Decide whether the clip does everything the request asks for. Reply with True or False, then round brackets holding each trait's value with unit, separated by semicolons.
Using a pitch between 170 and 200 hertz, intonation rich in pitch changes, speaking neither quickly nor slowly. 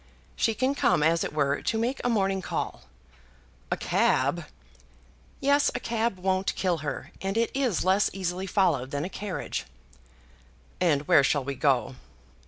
True (185 Hz; 6.9 semitones; 160 wpm)